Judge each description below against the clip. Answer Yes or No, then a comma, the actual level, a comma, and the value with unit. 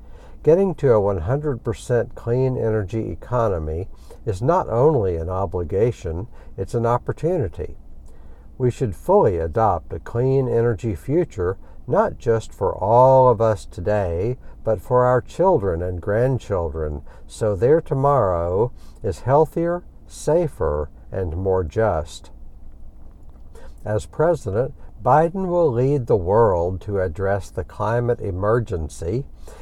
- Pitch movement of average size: No, wide, 6.8 semitones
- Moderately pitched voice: No, low, 105 Hz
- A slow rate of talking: Yes, slow, 115 wpm